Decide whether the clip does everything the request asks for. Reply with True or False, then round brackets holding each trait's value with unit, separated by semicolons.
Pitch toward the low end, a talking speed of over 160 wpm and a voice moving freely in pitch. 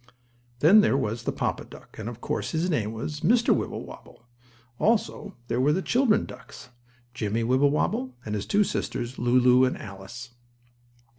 False (130 Hz; 155 wpm; 5.9 semitones)